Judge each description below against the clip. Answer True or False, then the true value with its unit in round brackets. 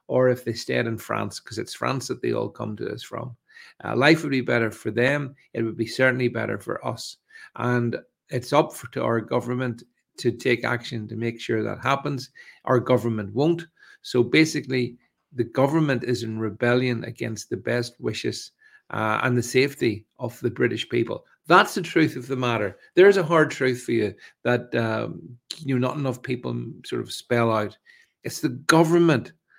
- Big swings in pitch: False (3.0 semitones)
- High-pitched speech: False (125 Hz)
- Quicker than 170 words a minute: True (190 wpm)